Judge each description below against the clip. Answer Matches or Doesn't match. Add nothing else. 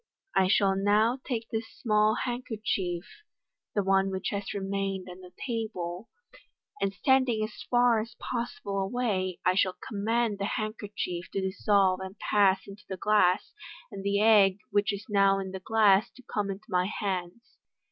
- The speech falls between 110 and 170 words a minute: Matches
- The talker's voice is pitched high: Matches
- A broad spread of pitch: Doesn't match